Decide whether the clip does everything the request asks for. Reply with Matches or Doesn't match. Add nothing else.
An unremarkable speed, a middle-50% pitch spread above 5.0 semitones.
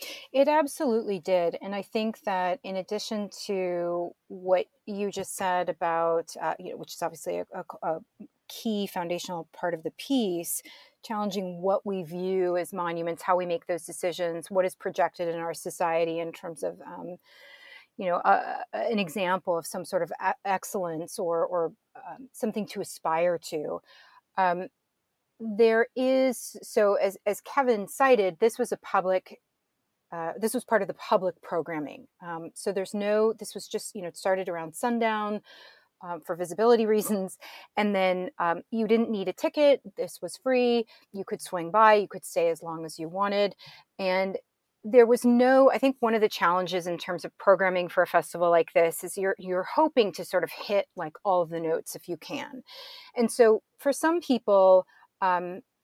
Doesn't match